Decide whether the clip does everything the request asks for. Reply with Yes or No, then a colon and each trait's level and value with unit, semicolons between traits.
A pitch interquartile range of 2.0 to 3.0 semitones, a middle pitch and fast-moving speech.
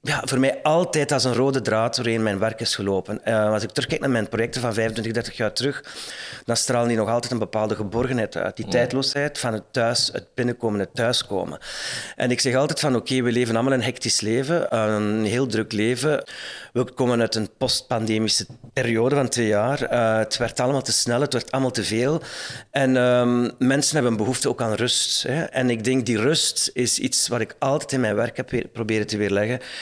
No: average, 2.7 semitones; low, 120 Hz; fast, 215 wpm